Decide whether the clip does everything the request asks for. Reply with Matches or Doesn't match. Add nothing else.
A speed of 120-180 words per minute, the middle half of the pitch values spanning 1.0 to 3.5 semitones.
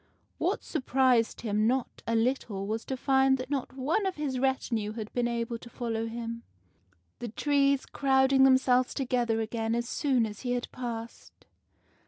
Matches